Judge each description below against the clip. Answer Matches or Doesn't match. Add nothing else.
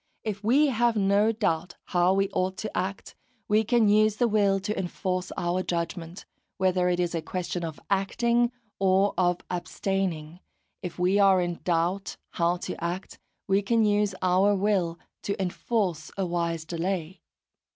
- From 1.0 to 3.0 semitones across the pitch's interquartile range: Matches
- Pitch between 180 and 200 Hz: Matches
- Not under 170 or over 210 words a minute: Doesn't match